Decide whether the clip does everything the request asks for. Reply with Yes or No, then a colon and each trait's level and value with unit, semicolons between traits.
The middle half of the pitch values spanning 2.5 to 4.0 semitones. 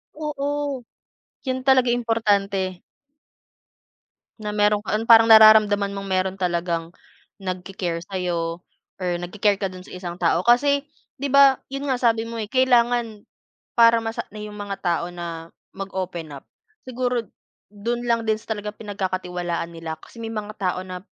No: average, 4.4 semitones